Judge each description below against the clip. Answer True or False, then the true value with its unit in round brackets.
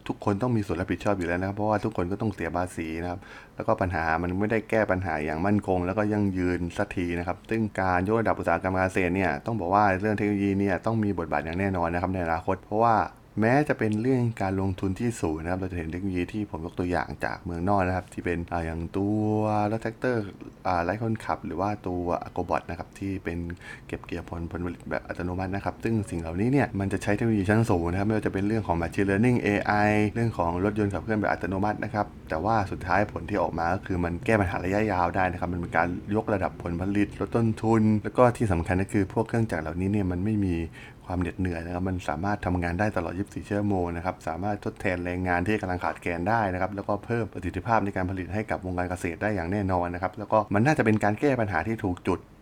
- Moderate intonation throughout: True (3.3 semitones)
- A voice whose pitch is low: True (95 Hz)